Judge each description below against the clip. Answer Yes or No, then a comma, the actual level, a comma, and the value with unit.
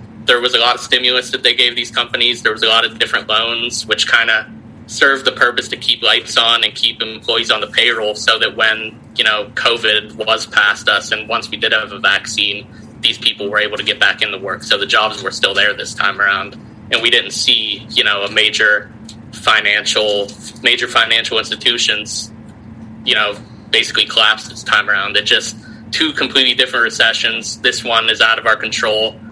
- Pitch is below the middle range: Yes, low, 110 Hz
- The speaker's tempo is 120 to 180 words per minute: No, fast, 205 wpm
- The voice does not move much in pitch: Yes, narrow, 1.5 semitones